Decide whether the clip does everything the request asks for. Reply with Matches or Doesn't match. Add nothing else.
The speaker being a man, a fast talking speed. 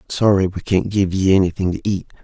Matches